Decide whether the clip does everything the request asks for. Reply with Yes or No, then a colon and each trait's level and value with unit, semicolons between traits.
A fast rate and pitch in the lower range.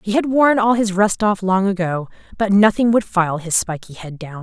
No: fast, 230 wpm; high, 200 Hz